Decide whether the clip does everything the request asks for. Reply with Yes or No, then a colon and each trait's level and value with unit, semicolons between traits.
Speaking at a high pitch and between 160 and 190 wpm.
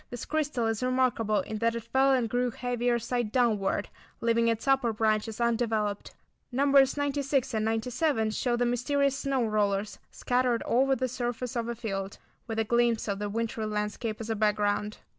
Yes: high, 235 Hz; average, 175 wpm